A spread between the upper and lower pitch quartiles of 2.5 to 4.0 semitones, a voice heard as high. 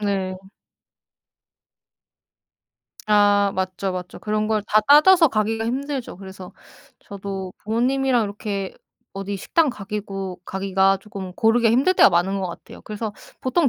Yes: average, 3.2 semitones; high, 205 Hz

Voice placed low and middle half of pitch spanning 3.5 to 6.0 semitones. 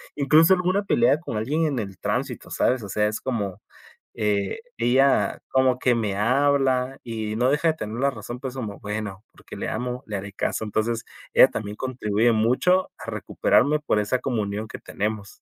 Yes: low, 120 Hz; average, 4.2 semitones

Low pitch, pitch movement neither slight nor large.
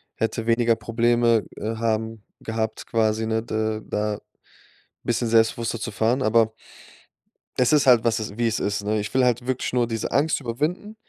No: low, 115 Hz; narrow, 1.5 semitones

